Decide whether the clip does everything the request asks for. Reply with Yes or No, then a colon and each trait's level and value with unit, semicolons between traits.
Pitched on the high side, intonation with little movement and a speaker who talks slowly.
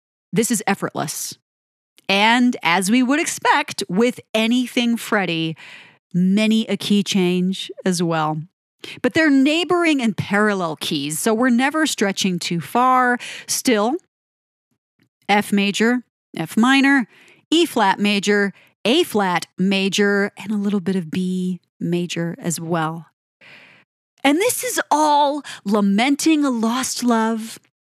No: high, 205 Hz; wide, 5.4 semitones; slow, 125 wpm